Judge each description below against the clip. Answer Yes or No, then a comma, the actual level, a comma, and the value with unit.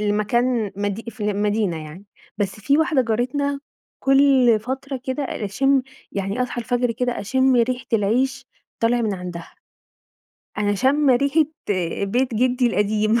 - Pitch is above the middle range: Yes, high, 240 Hz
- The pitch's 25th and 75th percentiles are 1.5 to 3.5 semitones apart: No, average, 4.0 semitones